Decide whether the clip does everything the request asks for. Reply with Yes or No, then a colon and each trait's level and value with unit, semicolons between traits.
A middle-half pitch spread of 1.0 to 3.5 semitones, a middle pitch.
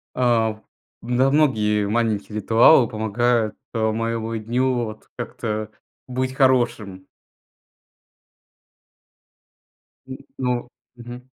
No: narrow, 2.6 semitones; low, 115 Hz